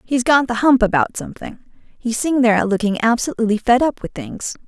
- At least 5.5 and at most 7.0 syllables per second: Yes, 5.9 syllables/s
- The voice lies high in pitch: Yes, high, 235 Hz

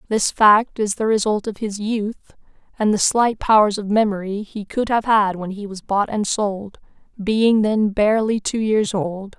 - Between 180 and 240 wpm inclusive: Yes, average, 190 wpm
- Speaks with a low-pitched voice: No, high, 210 Hz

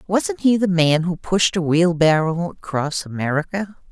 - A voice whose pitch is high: No, medium, 175 Hz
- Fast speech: No, average, 155 wpm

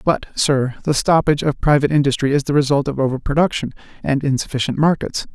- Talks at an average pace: Yes, average, 180 wpm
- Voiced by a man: Yes, male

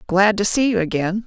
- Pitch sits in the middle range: No, high, 200 Hz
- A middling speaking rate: No, fast, 235 wpm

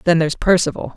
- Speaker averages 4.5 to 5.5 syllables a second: No, 7.2 syllables/s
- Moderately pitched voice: Yes, medium, 165 Hz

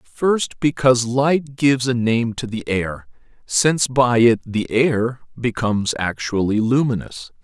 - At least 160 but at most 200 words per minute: No, slow, 135 wpm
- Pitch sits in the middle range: No, low, 120 Hz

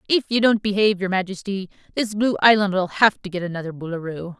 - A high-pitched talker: Yes, high, 195 Hz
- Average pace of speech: Yes, average, 190 wpm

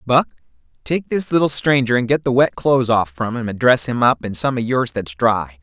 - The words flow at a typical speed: No, fast, 245 wpm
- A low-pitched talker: Yes, low, 120 Hz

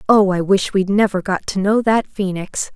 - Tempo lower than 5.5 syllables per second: Yes, 4.7 syllables/s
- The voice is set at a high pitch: Yes, high, 195 Hz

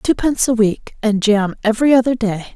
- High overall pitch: Yes, high, 225 Hz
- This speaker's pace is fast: No, average, 190 wpm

